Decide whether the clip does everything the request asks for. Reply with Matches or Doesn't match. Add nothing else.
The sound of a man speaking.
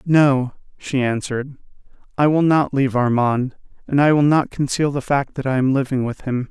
Matches